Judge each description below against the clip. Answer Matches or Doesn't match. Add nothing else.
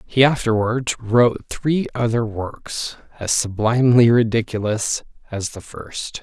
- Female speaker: Doesn't match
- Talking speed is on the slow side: Matches